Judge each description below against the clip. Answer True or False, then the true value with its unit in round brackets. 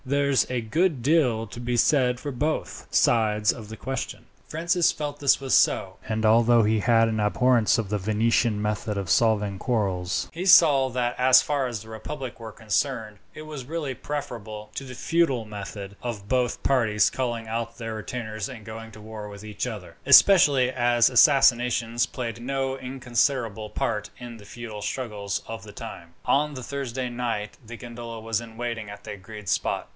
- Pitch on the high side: False (115 Hz)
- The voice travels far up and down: False (3.3 semitones)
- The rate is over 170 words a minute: True (180 wpm)